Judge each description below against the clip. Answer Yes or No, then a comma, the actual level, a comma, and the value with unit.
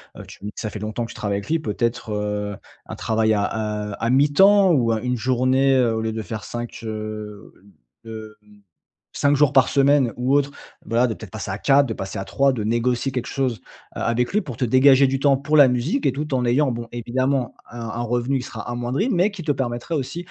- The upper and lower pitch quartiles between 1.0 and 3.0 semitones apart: No, average, 3.7 semitones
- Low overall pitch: Yes, low, 120 Hz